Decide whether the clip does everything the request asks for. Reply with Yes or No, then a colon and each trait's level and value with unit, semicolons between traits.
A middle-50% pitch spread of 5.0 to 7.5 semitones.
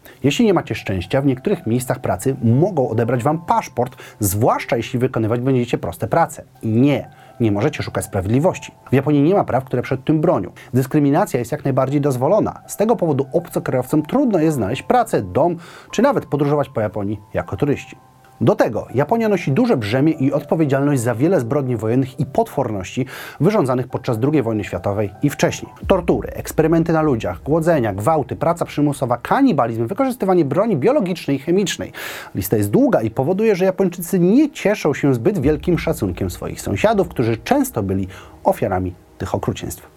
Yes: wide, 5.6 semitones